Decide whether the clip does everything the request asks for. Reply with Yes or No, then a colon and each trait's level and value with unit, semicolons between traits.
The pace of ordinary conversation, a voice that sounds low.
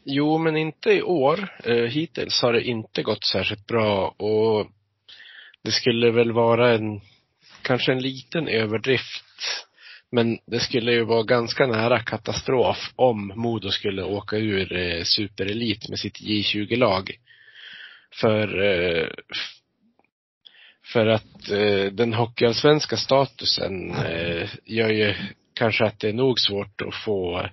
No: slow, 120 wpm; low, 115 Hz